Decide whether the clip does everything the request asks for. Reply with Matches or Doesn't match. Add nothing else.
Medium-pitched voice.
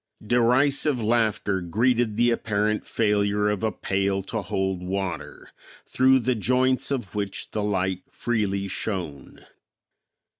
Doesn't match